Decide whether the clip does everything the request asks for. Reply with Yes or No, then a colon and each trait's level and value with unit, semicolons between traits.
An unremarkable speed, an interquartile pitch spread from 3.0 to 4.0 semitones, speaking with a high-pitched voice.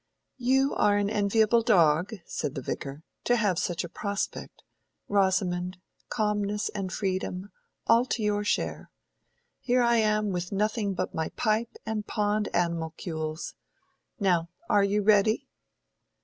No: slow, 130 wpm; average, 3.3 semitones; high, 205 Hz